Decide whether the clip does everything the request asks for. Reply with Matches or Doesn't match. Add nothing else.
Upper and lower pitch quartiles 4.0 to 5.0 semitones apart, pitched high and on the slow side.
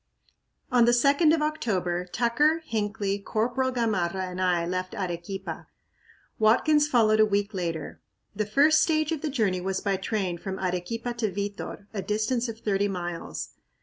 Doesn't match